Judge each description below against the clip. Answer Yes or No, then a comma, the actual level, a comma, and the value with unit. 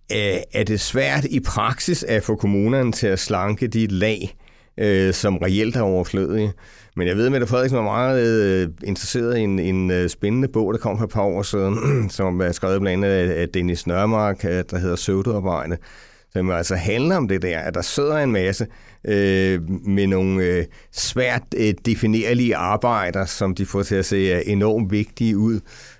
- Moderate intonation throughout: Yes, average, 3.2 semitones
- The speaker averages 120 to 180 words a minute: Yes, average, 165 wpm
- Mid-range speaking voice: No, low, 100 Hz